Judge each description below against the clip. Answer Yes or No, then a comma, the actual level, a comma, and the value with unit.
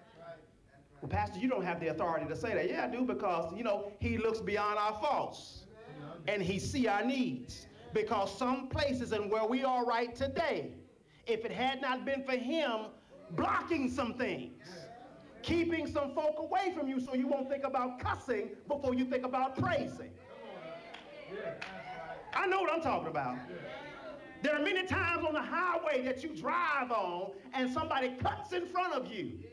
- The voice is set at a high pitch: Yes, very high, 255 Hz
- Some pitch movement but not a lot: No, wide, 5.8 semitones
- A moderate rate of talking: Yes, average, 175 wpm